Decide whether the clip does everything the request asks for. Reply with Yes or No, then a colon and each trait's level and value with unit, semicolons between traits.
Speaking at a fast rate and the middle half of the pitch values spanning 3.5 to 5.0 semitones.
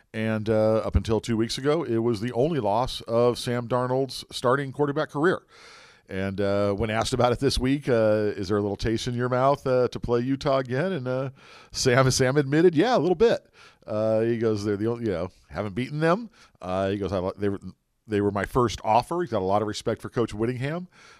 Yes: fast, 220 wpm; average, 4.0 semitones